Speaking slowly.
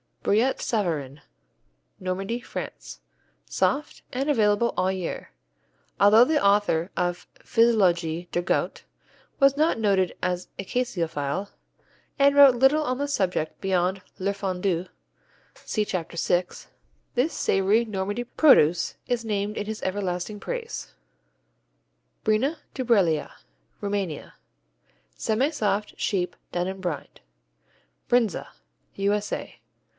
Yes: slow, 110 wpm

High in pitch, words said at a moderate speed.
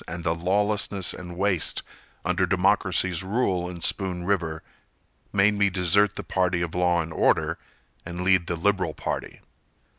No: very low, 90 Hz; average, 150 wpm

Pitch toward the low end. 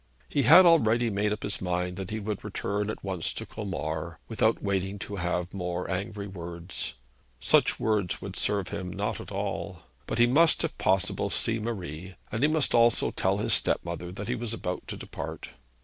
Yes: low, 100 Hz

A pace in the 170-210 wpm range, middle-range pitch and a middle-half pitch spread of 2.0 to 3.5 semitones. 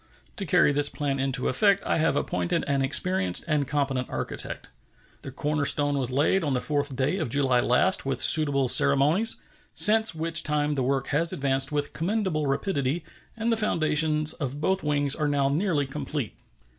Yes: average, 175 wpm; medium, 145 Hz; average, 2.9 semitones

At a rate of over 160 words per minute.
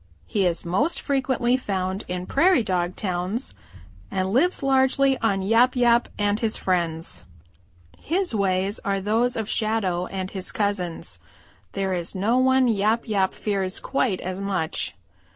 No: average, 145 wpm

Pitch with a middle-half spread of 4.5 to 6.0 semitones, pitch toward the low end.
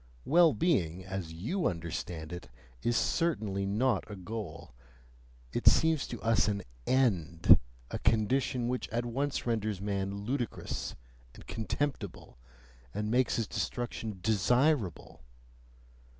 Yes: average, 4.8 semitones; low, 110 Hz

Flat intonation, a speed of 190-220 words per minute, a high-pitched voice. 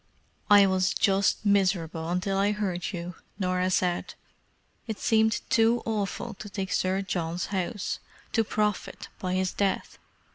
No: narrow, 2.3 semitones; slow, 135 wpm; high, 195 Hz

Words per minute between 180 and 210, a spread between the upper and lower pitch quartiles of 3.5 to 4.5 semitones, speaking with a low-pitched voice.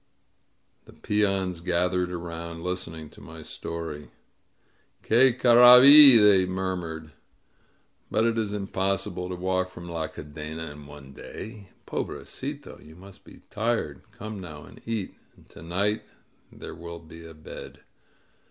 No: average, 145 wpm; average, 4.1 semitones; very low, 90 Hz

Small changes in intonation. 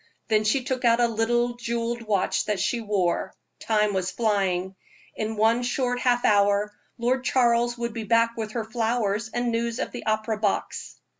Yes: narrow, 2.1 semitones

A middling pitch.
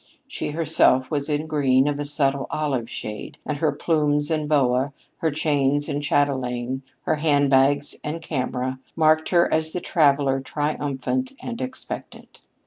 Yes: medium, 145 Hz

